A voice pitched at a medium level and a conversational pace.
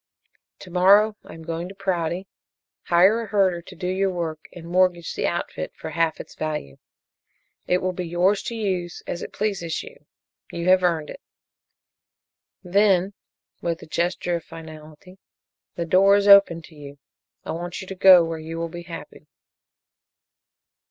Yes: medium, 175 Hz; average, 165 wpm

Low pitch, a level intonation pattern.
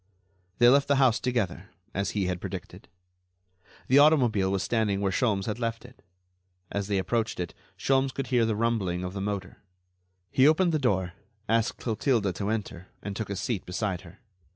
No: low, 110 Hz; average, 4.3 semitones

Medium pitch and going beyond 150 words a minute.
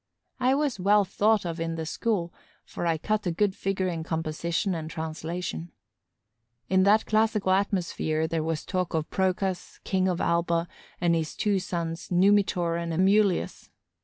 Yes: medium, 180 Hz; average, 160 wpm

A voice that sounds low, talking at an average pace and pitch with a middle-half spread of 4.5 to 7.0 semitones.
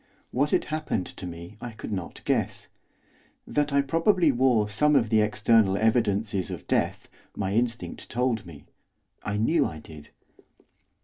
Yes: low, 110 Hz; average, 150 wpm; average, 5.2 semitones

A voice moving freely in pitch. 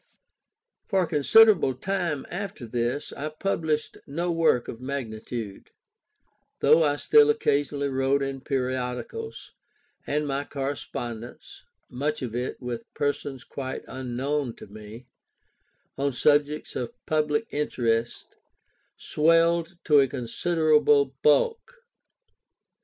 No: average, 3.7 semitones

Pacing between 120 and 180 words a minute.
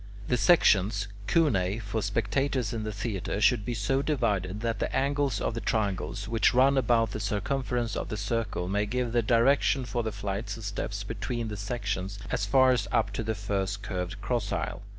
No: average, 190 wpm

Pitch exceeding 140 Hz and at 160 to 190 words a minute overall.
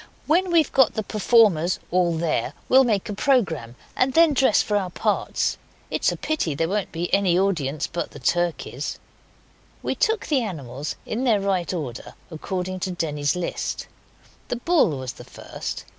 Yes: medium, 185 Hz; average, 170 wpm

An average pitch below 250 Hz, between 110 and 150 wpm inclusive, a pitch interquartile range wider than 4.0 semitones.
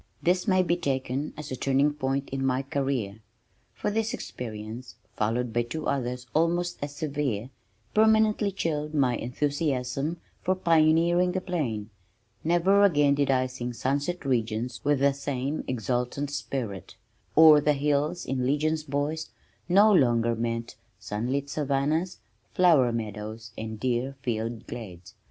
Yes: medium, 140 Hz; average, 140 wpm; average, 4.4 semitones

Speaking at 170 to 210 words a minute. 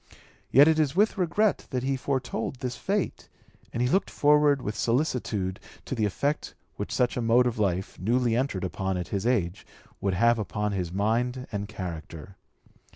Yes: average, 175 wpm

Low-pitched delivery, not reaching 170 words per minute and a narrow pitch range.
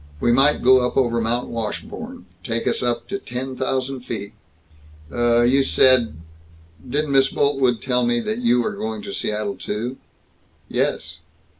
Yes: low, 125 Hz; average, 155 wpm; narrow, 2.3 semitones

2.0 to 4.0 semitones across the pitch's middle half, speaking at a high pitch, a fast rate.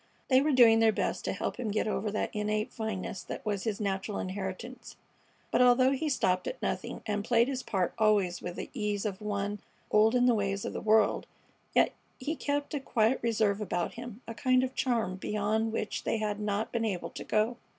Yes: average, 3.0 semitones; high, 215 Hz; fast, 210 wpm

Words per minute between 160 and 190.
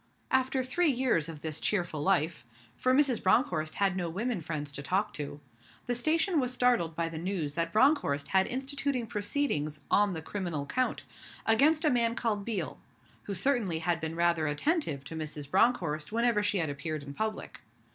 Yes: average, 175 wpm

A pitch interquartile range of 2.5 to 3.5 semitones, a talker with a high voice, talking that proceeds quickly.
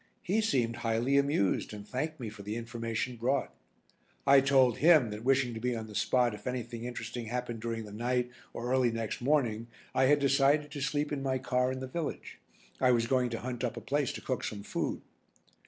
No: average, 2.9 semitones; low, 125 Hz; fast, 210 wpm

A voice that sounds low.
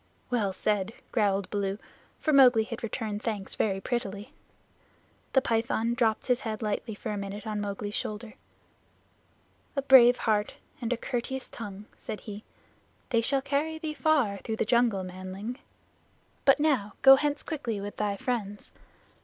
No: high, 225 Hz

